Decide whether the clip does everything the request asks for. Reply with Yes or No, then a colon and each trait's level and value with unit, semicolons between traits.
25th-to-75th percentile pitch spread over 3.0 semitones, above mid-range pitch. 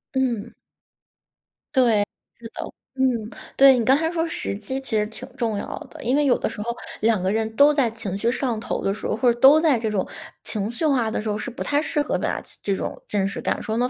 Yes: average, 3.9 semitones; high, 235 Hz